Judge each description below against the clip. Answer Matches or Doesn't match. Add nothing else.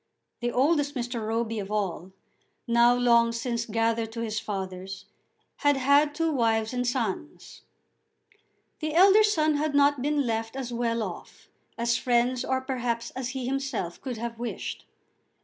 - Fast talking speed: Doesn't match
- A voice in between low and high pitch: Doesn't match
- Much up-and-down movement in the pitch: Doesn't match